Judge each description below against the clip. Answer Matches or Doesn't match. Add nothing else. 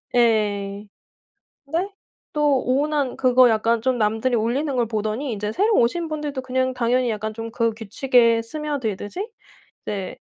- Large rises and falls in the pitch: Doesn't match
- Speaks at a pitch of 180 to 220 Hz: Doesn't match